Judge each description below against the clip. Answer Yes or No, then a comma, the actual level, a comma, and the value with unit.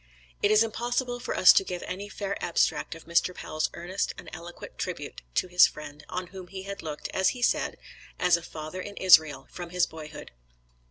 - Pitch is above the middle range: No, medium, 180 Hz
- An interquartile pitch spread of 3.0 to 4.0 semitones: Yes, average, 3.3 semitones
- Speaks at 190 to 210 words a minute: Yes, average, 195 wpm